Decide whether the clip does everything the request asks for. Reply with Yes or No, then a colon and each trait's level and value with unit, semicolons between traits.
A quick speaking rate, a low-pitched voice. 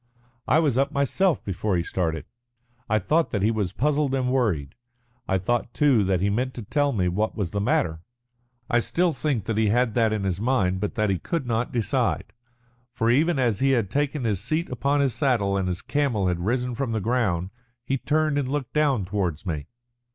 Yes: fast, 210 wpm; low, 115 Hz